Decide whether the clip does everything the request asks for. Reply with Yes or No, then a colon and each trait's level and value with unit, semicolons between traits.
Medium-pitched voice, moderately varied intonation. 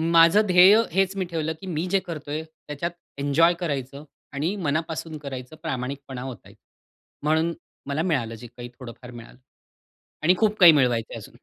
Yes: medium, 155 Hz; average, 4.3 semitones